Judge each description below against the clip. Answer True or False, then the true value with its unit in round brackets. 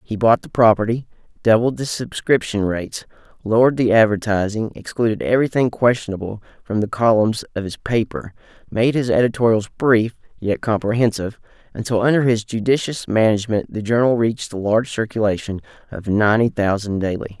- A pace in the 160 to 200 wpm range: False (140 wpm)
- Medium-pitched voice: False (110 Hz)